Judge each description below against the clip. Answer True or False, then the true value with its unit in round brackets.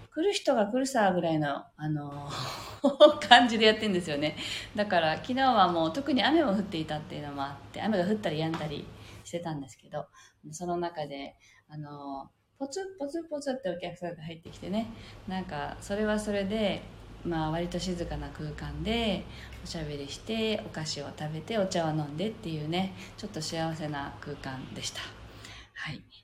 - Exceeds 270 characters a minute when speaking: True (350 characters per minute)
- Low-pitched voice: False (170 Hz)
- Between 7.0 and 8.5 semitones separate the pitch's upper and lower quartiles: False (6.0 semitones)